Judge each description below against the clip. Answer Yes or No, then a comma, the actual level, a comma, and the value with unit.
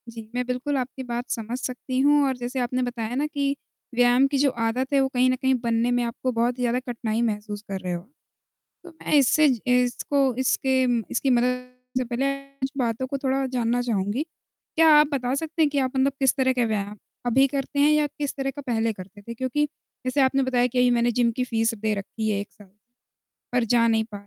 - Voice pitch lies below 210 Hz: No, very high, 250 Hz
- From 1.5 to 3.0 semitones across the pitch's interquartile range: Yes, narrow, 2.5 semitones